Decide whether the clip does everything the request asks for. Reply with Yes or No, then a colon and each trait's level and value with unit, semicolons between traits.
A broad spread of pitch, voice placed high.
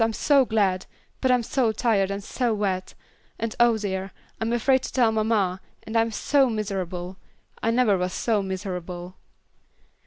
No: average, 3.5 semitones; high, 215 Hz